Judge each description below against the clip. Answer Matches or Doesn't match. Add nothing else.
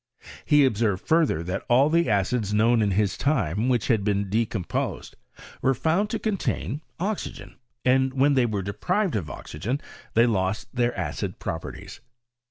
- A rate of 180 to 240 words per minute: Doesn't match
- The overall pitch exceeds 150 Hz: Doesn't match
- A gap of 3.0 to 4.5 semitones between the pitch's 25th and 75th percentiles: Doesn't match